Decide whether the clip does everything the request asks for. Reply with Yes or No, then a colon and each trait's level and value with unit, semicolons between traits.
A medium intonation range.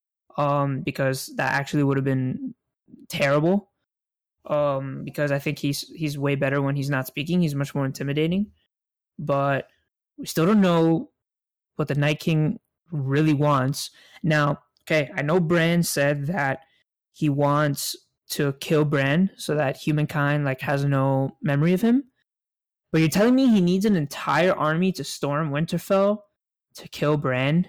Yes: average, 3.4 semitones